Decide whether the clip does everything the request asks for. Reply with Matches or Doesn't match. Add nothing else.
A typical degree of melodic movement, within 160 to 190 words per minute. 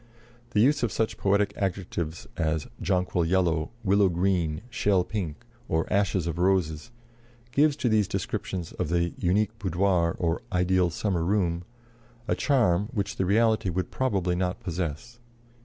Doesn't match